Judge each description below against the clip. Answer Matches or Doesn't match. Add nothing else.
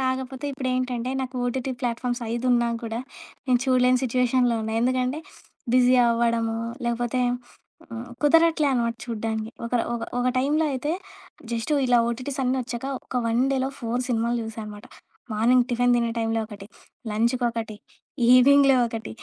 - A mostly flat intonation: Matches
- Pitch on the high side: Matches